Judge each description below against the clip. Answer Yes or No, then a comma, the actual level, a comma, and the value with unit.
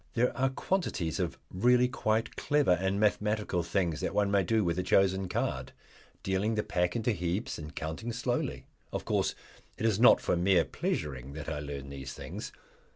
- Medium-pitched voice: No, very low, 95 Hz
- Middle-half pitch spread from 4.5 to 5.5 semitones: Yes, average, 4.8 semitones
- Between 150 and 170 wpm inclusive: No, average, 180 wpm